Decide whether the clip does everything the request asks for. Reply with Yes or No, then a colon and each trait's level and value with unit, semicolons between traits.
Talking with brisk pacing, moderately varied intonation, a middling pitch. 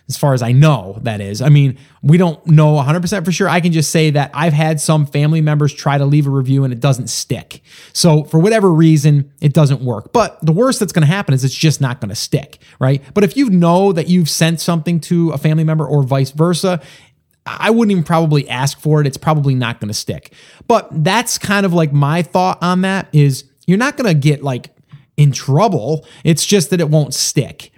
Yes: fast, 235 wpm; average, 3.6 semitones; medium, 155 Hz